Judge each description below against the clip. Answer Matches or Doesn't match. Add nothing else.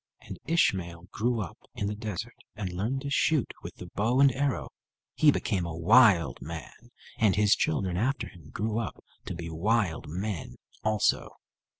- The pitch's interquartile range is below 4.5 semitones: Doesn't match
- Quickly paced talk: Doesn't match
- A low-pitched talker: Matches